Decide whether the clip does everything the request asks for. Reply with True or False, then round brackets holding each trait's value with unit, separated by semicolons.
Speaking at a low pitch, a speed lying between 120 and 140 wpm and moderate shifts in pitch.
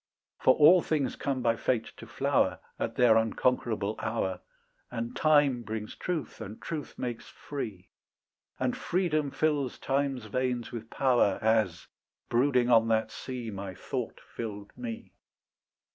True (120 Hz; 135 wpm; 3.6 semitones)